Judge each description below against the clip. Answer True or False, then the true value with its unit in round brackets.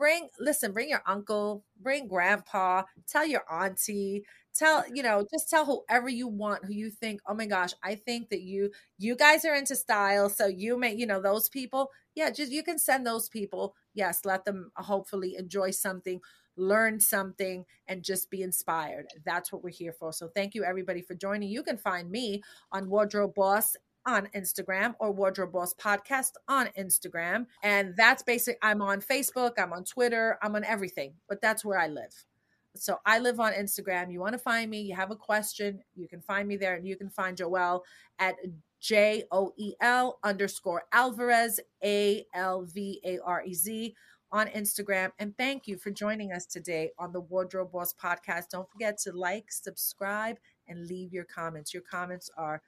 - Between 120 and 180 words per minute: False (190 wpm)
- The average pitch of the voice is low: False (200 Hz)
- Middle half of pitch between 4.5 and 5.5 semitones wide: False (3.2 semitones)